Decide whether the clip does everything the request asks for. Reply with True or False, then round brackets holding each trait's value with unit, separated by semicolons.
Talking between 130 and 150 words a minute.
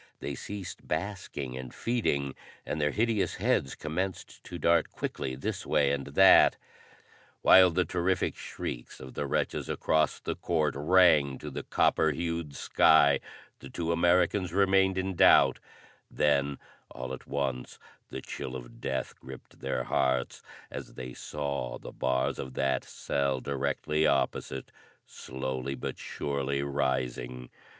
True (140 wpm)